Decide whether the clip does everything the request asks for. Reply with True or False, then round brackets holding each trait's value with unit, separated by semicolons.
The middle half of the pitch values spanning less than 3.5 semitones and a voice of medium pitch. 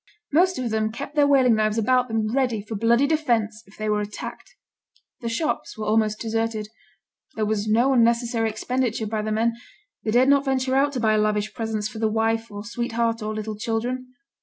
False (2.7 semitones; 225 Hz)